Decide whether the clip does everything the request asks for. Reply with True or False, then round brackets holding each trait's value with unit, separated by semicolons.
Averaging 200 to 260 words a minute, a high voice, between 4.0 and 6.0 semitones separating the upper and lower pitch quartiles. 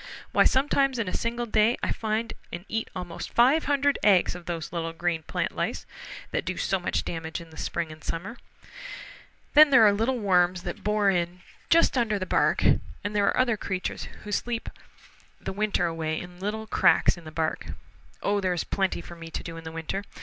True (205 wpm; 195 Hz; 4.7 semitones)